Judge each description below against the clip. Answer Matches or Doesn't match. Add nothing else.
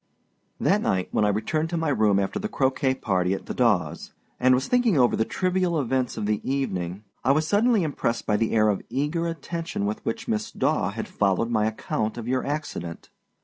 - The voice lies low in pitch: Matches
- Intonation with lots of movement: Matches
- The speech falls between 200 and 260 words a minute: Matches